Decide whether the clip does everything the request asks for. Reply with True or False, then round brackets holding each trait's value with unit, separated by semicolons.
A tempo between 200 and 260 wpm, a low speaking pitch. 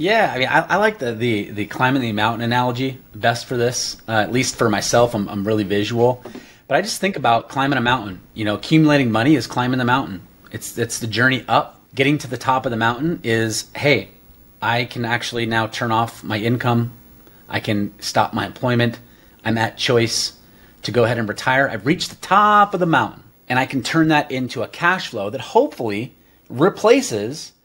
True (205 wpm; 120 Hz)